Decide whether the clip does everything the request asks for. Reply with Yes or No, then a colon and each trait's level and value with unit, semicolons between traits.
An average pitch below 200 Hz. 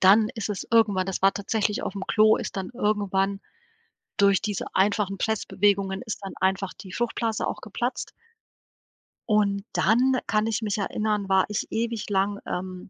No: high, 205 Hz